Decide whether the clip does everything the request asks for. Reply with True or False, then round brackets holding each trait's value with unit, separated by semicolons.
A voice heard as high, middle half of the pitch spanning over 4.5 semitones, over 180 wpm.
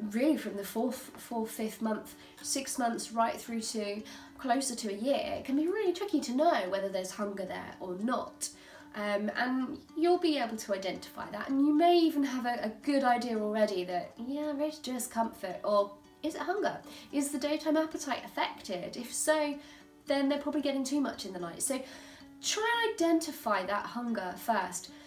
True (260 Hz; 5.5 semitones; 190 wpm)